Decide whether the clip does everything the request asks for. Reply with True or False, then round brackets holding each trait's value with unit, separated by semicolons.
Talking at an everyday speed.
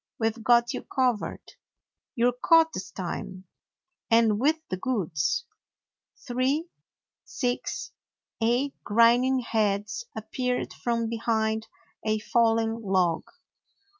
False (105 wpm)